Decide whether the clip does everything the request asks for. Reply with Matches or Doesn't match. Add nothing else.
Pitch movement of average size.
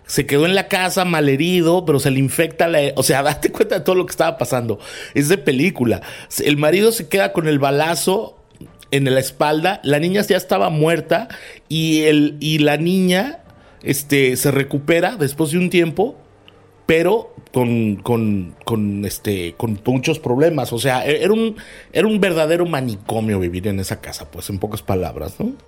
Doesn't match